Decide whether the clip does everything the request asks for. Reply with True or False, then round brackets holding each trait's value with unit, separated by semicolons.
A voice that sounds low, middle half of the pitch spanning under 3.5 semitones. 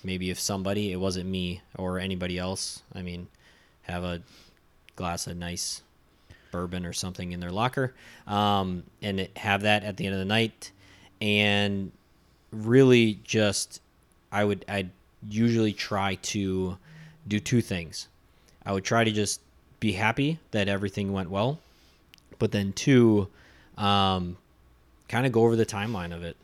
True (100 Hz; 2.8 semitones)